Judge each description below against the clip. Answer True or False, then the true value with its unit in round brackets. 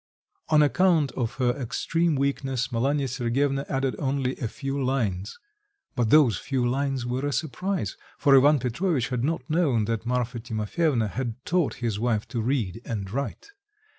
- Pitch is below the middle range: True (130 Hz)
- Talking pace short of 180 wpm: True (160 wpm)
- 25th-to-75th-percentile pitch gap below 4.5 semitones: True (3.4 semitones)